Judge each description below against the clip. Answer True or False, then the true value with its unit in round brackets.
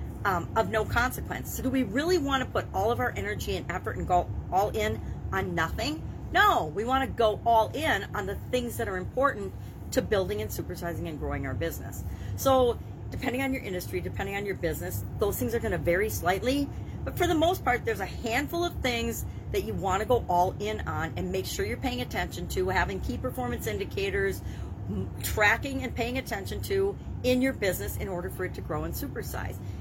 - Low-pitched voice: False (190 Hz)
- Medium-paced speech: False (210 wpm)